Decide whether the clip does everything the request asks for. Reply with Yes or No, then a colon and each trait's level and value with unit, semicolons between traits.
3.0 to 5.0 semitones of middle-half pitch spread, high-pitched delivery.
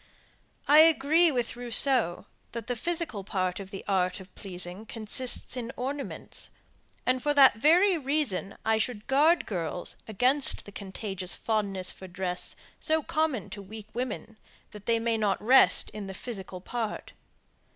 No: wide, 5.6 semitones; high, 225 Hz